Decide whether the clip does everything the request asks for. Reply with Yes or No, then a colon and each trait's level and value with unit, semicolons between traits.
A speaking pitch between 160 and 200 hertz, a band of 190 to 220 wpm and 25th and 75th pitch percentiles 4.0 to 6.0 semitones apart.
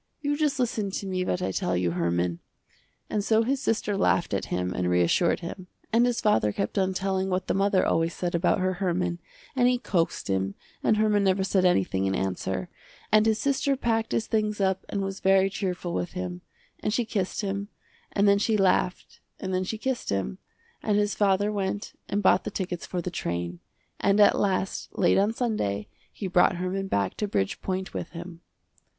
No: high, 190 Hz; average, 200 wpm; average, 3.3 semitones